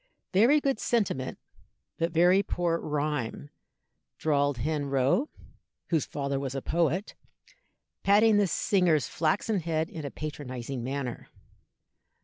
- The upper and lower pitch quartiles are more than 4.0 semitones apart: Yes, average, 4.9 semitones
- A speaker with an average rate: No, slow, 120 wpm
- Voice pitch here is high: No, medium, 155 Hz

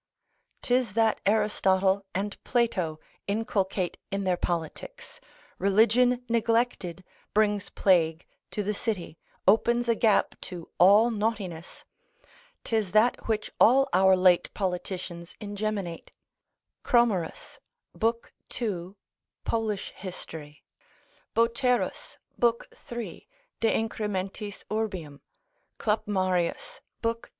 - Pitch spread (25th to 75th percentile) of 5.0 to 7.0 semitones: No, average, 3.5 semitones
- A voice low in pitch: No, high, 205 Hz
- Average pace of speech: No, slow, 95 wpm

